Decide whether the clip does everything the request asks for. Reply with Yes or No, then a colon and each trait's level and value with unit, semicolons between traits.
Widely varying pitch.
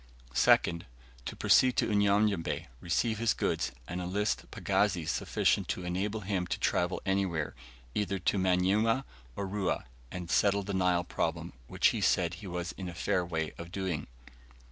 No: narrow, 2.6 semitones